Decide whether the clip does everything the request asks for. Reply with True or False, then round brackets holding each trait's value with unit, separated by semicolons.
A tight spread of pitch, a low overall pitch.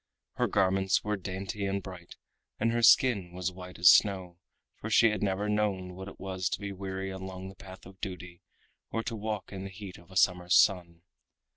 True (1.6 semitones; 95 Hz)